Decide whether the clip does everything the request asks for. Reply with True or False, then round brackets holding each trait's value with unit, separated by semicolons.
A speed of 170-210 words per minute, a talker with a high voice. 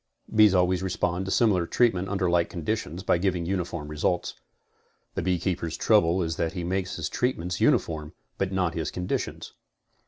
False (175 wpm; 90 Hz)